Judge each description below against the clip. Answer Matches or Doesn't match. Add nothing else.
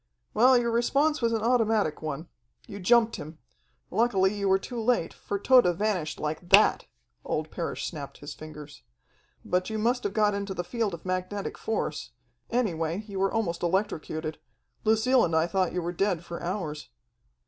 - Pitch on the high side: Matches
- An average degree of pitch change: Matches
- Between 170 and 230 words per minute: Matches